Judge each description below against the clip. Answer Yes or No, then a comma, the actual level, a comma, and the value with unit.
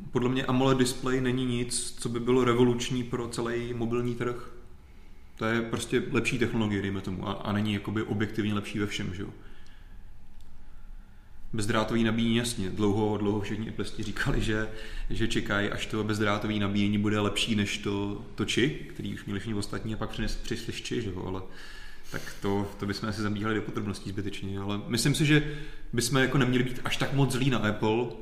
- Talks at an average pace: No, fast, 180 wpm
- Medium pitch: No, low, 110 Hz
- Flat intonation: No, average, 3.0 semitones